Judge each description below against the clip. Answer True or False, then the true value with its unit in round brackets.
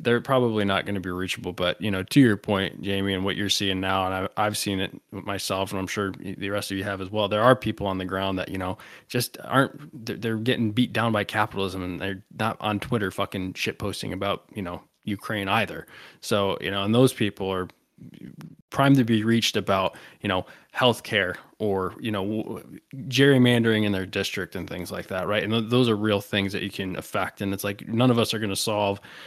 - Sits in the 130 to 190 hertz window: False (100 Hz)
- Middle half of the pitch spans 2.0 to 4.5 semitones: True (2.6 semitones)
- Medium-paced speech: False (230 wpm)